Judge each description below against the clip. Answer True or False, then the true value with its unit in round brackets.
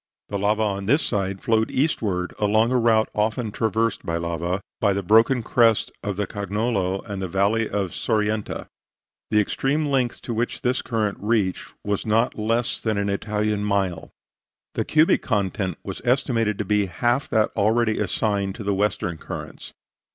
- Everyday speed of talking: True (165 wpm)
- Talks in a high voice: False (105 Hz)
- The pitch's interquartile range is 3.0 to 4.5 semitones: False (2.5 semitones)